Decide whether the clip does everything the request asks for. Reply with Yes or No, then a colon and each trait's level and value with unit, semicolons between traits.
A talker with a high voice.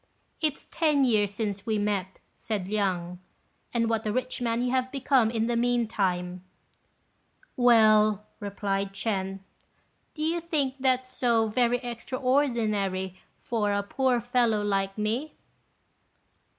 Yes: high, 225 Hz